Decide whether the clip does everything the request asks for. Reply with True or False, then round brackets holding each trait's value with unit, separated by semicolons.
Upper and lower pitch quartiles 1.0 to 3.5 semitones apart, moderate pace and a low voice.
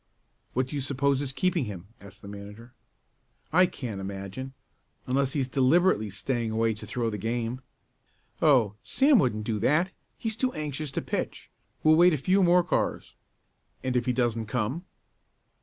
False (5.6 semitones; 170 wpm; 130 Hz)